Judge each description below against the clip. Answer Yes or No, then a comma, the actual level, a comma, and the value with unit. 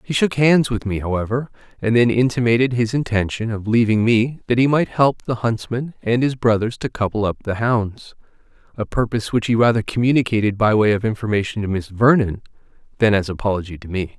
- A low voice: Yes, low, 115 Hz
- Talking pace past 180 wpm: Yes, average, 190 wpm